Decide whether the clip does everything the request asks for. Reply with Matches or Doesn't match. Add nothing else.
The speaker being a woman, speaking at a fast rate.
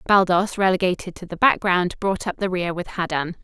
Doesn't match